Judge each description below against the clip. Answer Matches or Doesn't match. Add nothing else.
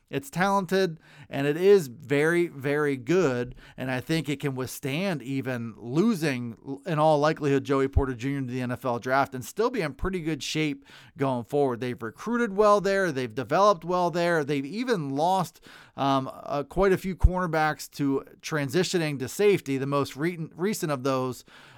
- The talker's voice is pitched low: Doesn't match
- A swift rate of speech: Doesn't match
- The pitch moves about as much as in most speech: Matches